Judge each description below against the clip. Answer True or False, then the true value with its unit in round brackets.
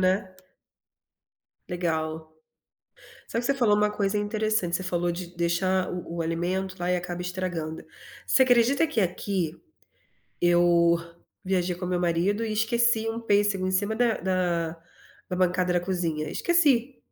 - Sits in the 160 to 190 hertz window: True (185 Hz)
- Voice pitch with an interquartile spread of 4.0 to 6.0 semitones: False (3.4 semitones)